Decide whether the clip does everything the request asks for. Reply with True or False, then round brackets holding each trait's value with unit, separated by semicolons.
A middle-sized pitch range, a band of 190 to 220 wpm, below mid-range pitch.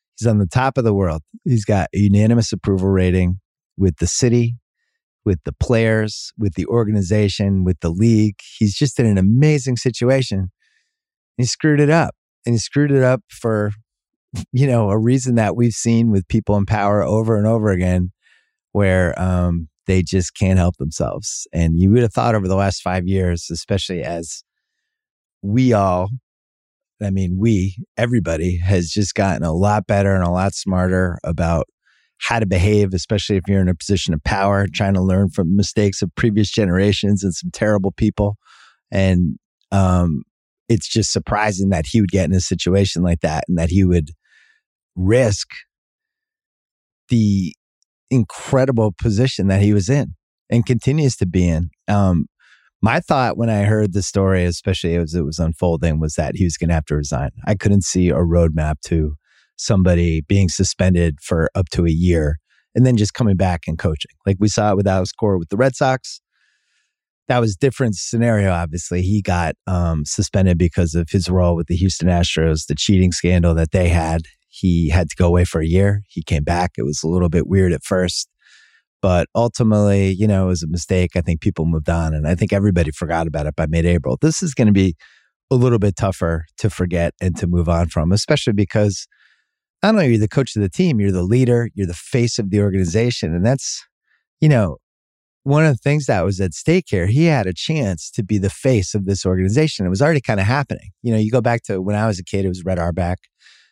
True (4.1 semitones; 200 wpm; 100 Hz)